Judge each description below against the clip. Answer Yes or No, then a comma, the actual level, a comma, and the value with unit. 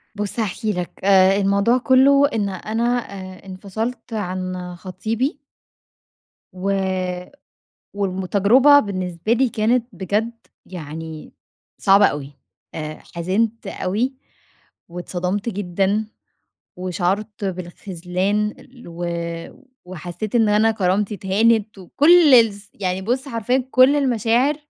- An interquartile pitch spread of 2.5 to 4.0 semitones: Yes, average, 3.7 semitones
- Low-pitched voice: No, high, 200 Hz